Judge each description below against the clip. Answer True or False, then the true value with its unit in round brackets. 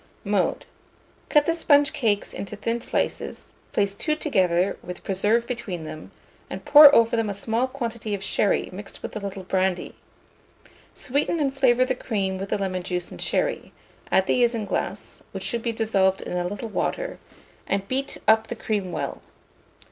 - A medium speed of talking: True (170 wpm)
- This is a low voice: False (220 Hz)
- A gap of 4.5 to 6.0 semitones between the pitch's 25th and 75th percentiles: True (4.8 semitones)